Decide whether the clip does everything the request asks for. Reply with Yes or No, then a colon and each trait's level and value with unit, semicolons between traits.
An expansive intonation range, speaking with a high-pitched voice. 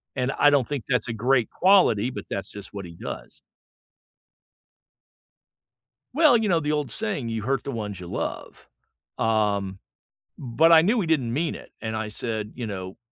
No: wide, 6.1 semitones; low, 120 Hz